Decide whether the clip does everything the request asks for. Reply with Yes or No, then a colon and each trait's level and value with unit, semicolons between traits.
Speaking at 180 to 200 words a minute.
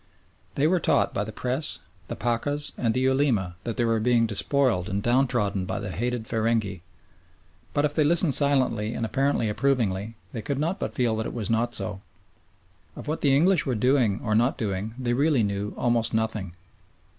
Yes: average, 190 wpm